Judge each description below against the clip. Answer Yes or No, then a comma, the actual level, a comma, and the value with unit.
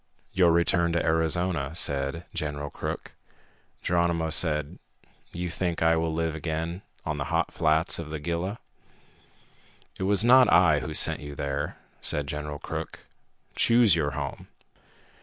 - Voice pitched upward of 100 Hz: No, very low, 80 Hz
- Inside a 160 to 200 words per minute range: No, average, 140 wpm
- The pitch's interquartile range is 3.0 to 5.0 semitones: No, narrow, 2.5 semitones